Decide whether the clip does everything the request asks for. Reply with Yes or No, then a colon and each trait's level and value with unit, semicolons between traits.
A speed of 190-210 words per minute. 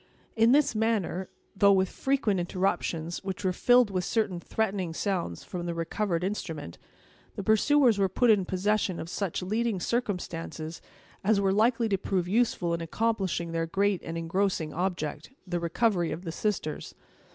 No: average, 155 wpm